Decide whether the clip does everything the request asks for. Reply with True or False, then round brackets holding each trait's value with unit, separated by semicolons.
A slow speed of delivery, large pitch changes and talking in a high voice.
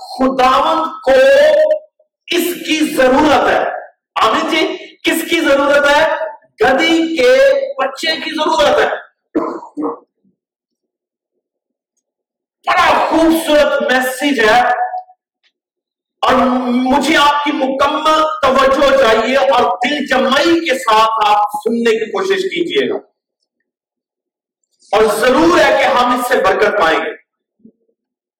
False (105 wpm; 3.7 semitones; 285 Hz)